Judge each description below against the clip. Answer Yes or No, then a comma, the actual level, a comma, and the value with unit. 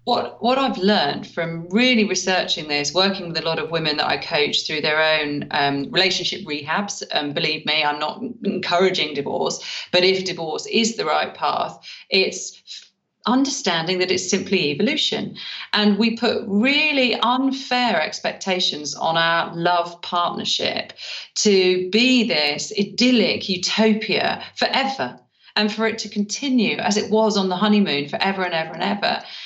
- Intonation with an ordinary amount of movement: Yes, average, 4.6 semitones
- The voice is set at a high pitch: Yes, high, 195 Hz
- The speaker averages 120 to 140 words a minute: No, average, 155 wpm